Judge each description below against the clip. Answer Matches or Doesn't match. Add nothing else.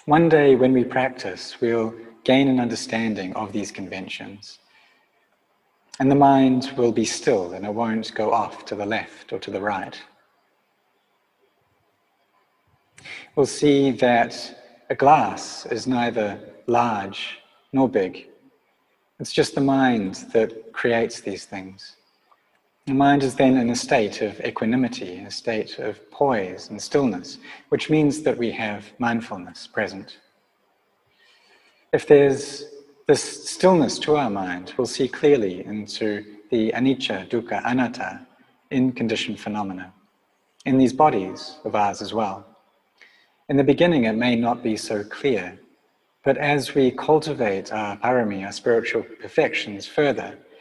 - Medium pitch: Doesn't match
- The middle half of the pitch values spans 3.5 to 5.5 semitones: Matches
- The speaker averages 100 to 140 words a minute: Matches